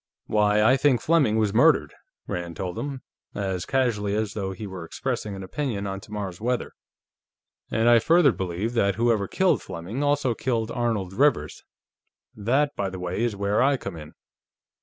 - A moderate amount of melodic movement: Yes, average, 4.6 semitones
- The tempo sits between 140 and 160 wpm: No, average, 170 wpm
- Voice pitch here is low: Yes, low, 105 Hz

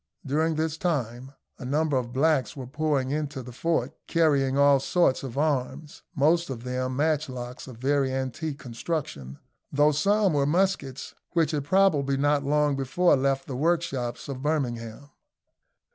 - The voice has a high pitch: No, medium, 140 Hz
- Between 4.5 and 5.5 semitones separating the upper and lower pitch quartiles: No, average, 3.2 semitones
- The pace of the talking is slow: No, average, 150 wpm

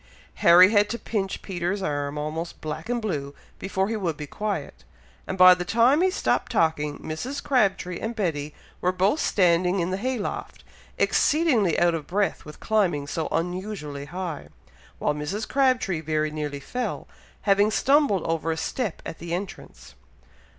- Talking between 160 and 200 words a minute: Yes, average, 165 wpm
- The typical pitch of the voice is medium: Yes, medium, 180 Hz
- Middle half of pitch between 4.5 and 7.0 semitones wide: Yes, average, 5.1 semitones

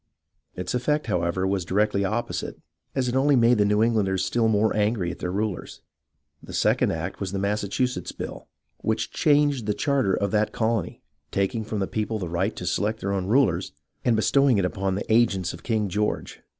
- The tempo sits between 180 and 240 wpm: Yes, average, 195 wpm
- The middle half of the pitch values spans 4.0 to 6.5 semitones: No, average, 3.4 semitones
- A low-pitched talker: Yes, low, 105 Hz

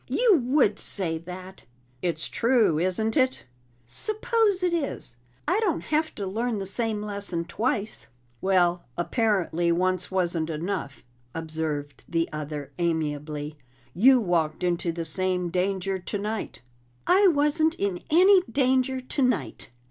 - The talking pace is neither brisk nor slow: No, slow, 125 wpm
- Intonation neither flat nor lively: No, wide, 7.2 semitones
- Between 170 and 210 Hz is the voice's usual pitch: Yes, high, 190 Hz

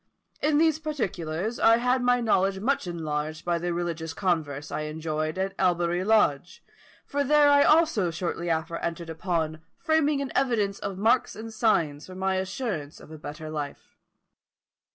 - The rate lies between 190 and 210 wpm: No, average, 160 wpm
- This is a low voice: No, medium, 180 Hz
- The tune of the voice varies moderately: No, wide, 6.5 semitones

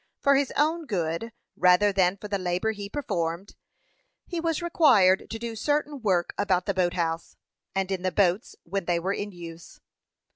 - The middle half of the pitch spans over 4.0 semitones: Yes, average, 4.5 semitones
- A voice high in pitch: Yes, high, 195 Hz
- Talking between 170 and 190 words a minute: Yes, average, 180 wpm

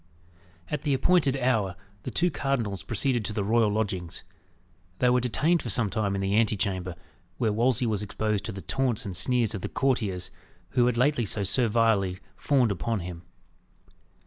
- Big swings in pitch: No, average, 4.3 semitones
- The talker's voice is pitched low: Yes, low, 110 Hz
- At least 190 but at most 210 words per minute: No, average, 175 wpm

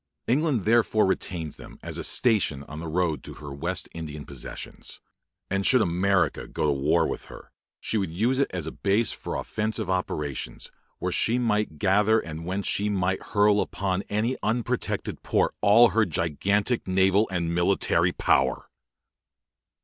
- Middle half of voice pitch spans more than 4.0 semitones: Yes, average, 4.6 semitones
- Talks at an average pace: Yes, average, 160 wpm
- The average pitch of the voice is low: Yes, very low, 95 Hz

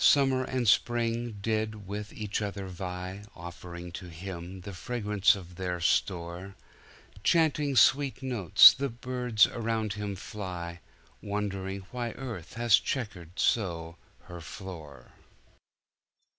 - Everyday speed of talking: No, slow, 115 wpm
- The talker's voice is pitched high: No, low, 100 Hz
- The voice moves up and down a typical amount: Yes, average, 4.7 semitones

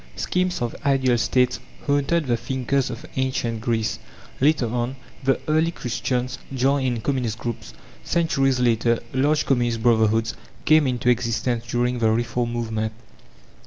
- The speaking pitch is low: Yes, low, 125 Hz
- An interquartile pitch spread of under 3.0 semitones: Yes, narrow, 2.6 semitones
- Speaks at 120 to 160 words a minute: Yes, slow, 135 wpm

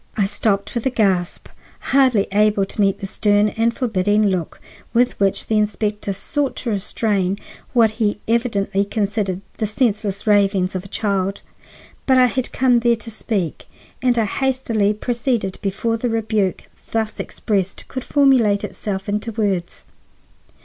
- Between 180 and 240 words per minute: No, average, 150 wpm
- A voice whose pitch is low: No, high, 210 Hz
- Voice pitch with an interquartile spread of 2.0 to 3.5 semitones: Yes, average, 2.8 semitones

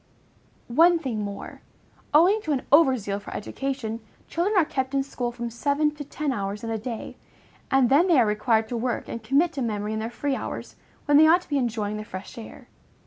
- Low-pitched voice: No, very high, 255 Hz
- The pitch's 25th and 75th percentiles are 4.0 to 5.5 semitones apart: Yes, average, 5.0 semitones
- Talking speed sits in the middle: No, fast, 215 wpm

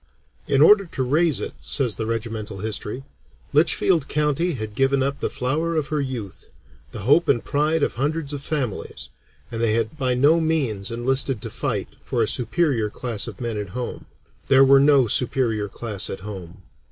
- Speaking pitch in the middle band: No, low, 130 Hz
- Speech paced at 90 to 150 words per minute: No, average, 180 wpm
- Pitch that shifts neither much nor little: Yes, average, 5.0 semitones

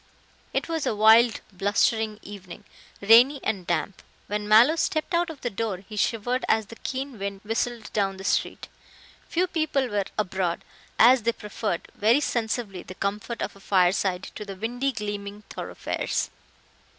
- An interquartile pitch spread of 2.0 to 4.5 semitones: Yes, average, 3.5 semitones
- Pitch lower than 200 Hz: No, high, 215 Hz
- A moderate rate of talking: Yes, average, 160 wpm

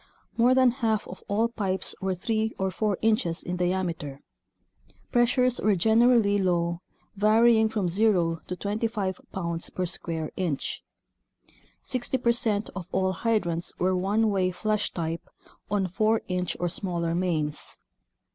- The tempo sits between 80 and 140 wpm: Yes, slow, 135 wpm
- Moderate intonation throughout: Yes, average, 4.0 semitones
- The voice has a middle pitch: No, high, 195 Hz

